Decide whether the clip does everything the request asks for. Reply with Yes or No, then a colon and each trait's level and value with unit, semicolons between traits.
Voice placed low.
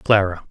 Yes: very low, 95 Hz